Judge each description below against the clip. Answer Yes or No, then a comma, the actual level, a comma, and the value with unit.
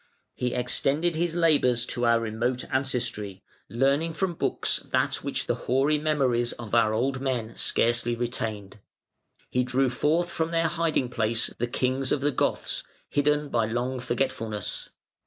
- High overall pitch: No, low, 125 Hz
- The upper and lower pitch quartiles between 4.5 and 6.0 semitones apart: No, average, 3.8 semitones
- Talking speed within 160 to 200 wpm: No, average, 150 wpm